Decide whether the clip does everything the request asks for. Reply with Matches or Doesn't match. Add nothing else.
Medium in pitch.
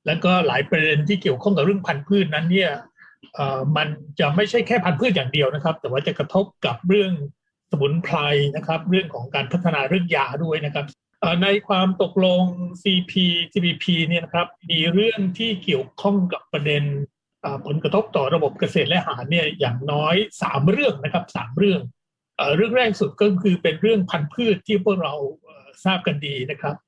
Matches